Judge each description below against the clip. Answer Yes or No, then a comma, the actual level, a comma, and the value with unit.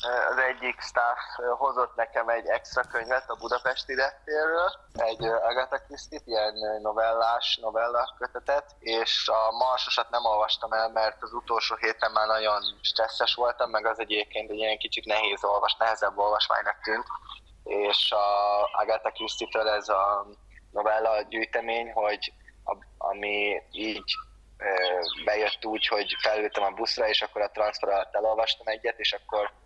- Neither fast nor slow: Yes, average, 140 wpm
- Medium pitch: No, low, 110 Hz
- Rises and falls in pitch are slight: Yes, narrow, 1.9 semitones